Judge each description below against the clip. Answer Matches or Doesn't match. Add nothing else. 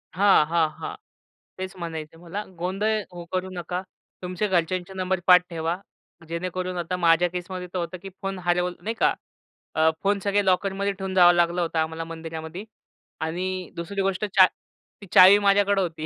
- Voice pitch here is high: Doesn't match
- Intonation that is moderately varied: Doesn't match